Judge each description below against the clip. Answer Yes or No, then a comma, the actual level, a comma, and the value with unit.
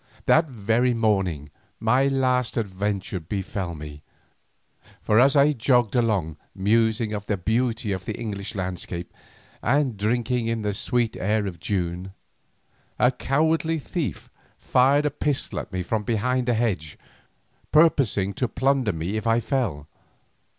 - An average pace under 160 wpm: Yes, average, 140 wpm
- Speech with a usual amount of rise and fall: Yes, average, 4.7 semitones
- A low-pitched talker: Yes, low, 110 Hz